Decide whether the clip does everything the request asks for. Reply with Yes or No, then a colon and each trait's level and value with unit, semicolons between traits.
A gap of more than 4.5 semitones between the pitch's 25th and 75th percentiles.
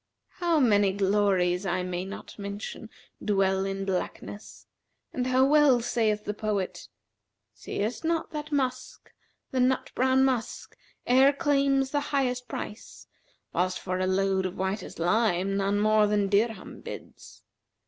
Yes: average, 5.0 semitones